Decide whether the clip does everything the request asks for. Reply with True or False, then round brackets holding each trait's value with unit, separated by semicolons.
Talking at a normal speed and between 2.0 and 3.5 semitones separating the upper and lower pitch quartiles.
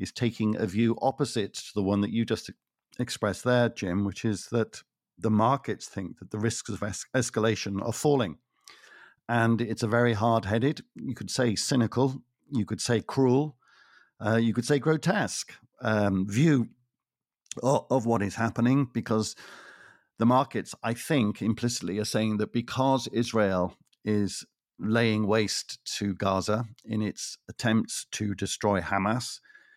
True (155 wpm; 2.8 semitones)